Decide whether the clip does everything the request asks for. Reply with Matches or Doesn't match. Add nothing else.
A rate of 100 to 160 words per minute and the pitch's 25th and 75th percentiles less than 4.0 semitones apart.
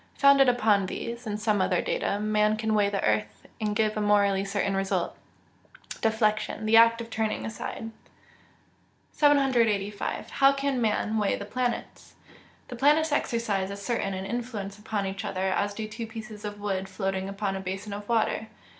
Doesn't match